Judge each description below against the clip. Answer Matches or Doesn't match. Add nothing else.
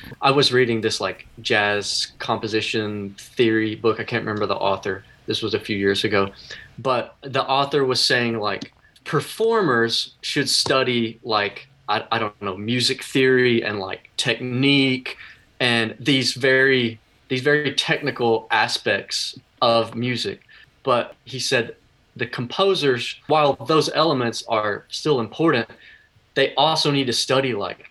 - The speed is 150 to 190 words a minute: Doesn't match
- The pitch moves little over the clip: Doesn't match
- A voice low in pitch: Matches